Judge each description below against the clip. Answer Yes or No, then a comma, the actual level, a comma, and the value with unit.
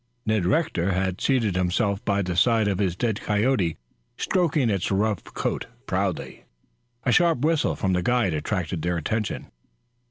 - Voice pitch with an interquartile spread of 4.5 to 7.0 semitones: Yes, average, 4.9 semitones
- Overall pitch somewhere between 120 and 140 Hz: No, low, 100 Hz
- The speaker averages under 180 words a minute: Yes, average, 155 wpm